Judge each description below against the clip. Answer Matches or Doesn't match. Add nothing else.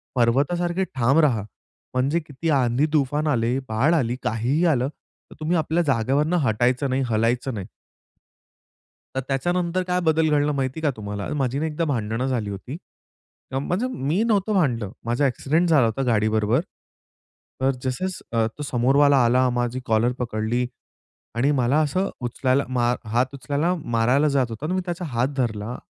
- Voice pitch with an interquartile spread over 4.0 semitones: Matches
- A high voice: Doesn't match